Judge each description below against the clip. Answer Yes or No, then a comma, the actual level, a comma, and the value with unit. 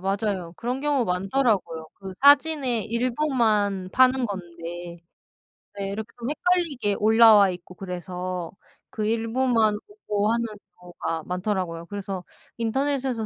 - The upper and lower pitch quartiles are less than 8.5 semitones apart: Yes, wide, 5.4 semitones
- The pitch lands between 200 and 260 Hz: Yes, high, 210 Hz